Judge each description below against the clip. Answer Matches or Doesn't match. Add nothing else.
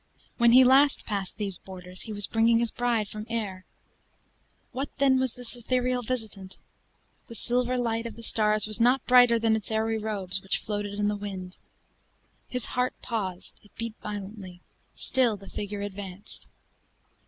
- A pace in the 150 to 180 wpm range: Matches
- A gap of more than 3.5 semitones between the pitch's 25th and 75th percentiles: Doesn't match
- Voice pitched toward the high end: Matches